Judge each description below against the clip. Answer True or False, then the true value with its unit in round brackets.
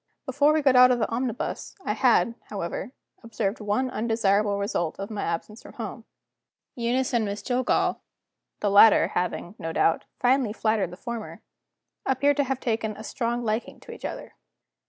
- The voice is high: True (225 Hz)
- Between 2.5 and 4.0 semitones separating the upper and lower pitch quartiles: True (3.6 semitones)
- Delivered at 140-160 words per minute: False (170 wpm)